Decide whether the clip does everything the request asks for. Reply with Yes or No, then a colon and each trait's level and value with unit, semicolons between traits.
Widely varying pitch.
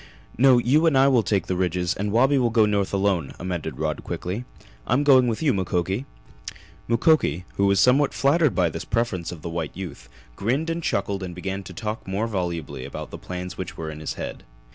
Yes: wide, 5.7 semitones